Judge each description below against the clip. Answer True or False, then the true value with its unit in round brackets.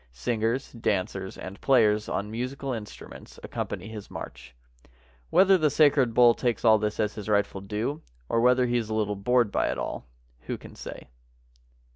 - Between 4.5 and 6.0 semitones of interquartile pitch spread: False (3.2 semitones)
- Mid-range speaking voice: False (110 Hz)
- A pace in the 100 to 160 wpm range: False (170 wpm)